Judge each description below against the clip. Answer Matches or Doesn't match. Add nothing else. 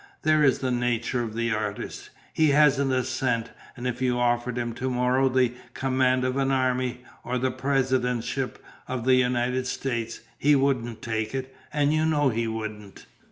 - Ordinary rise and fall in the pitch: Doesn't match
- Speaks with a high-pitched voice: Doesn't match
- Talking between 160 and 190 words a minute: Matches